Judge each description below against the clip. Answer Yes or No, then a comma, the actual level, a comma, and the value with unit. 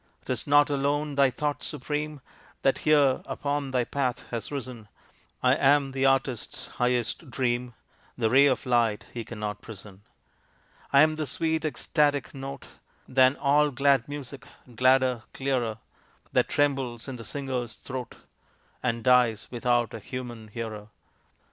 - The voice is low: Yes, low, 130 Hz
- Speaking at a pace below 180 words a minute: Yes, average, 140 wpm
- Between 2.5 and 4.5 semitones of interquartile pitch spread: Yes, average, 2.9 semitones